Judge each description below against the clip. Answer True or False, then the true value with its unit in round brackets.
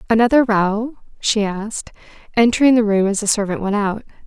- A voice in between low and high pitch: False (215 Hz)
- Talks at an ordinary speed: True (170 wpm)